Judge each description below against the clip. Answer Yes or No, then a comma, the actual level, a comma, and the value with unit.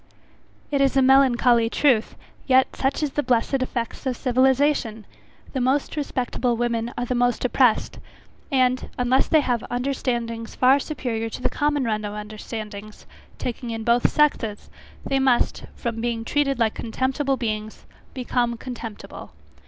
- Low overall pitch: No, high, 245 Hz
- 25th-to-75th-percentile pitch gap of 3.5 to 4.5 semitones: No, average, 2.7 semitones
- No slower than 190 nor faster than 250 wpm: No, average, 145 wpm